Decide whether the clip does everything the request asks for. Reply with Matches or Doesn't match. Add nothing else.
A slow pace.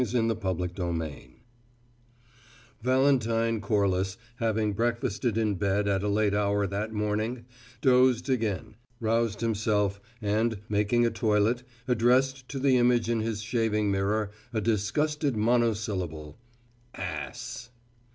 Matches